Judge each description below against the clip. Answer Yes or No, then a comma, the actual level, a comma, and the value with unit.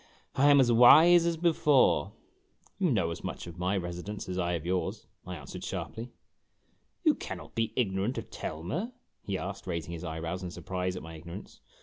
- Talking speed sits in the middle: No, fast, 215 wpm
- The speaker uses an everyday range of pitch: No, wide, 6.3 semitones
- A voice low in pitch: Yes, very low, 95 Hz